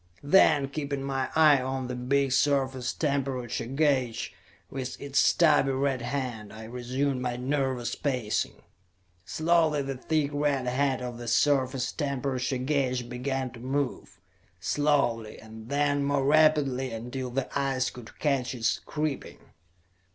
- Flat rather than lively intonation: Yes, narrow, 2.3 semitones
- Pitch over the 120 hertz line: Yes, low, 135 Hz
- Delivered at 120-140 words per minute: Yes, slow, 135 wpm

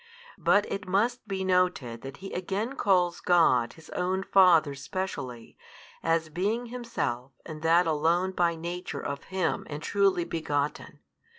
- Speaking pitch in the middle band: Yes, medium, 175 Hz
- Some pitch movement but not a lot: Yes, average, 3.9 semitones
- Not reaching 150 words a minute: Yes, average, 140 wpm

